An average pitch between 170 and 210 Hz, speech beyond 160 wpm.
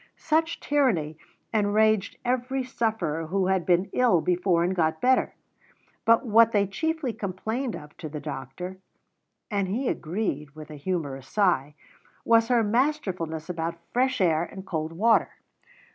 No: high, 190 Hz; average, 145 wpm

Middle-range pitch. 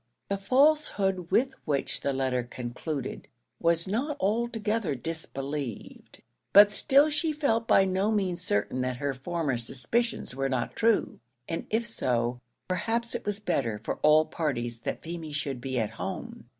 Yes: medium, 170 Hz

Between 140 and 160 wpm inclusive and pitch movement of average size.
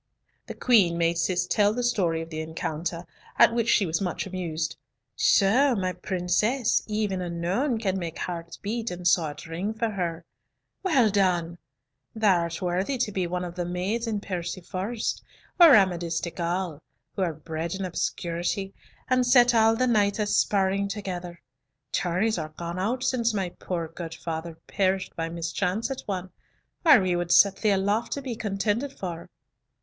No: average, 170 wpm; average, 4.2 semitones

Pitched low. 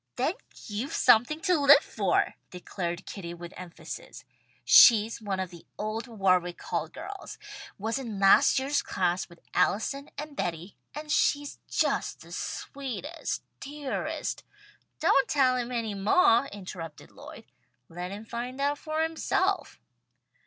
No: high, 230 Hz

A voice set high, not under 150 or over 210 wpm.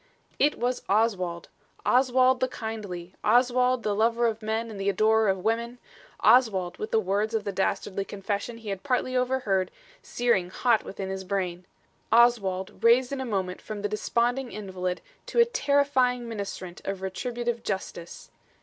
Yes: high, 220 Hz; average, 160 wpm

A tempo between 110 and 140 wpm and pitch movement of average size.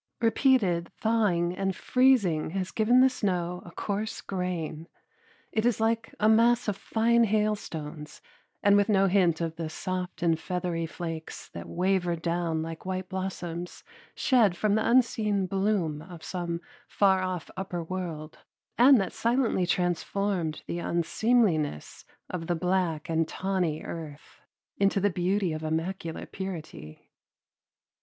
Yes: slow, 135 wpm; average, 3.7 semitones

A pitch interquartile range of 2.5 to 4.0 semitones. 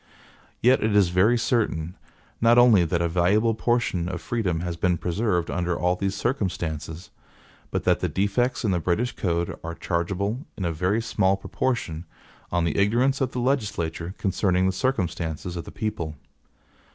No: average, 4.9 semitones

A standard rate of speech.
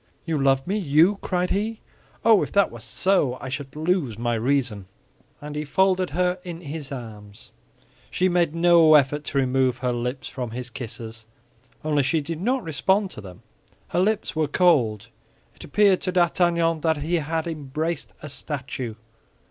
Yes: average, 170 wpm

